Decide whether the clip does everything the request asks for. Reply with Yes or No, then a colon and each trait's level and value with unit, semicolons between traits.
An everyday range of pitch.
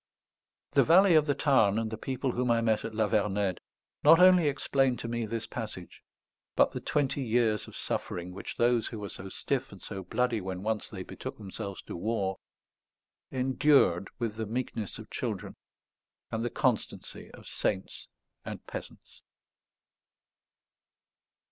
Yes: average, 4.2 semitones